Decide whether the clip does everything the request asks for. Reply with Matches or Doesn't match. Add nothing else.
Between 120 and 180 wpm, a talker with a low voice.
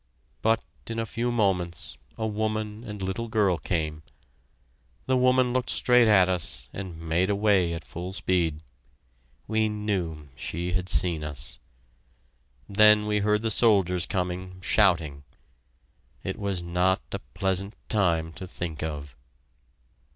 Matches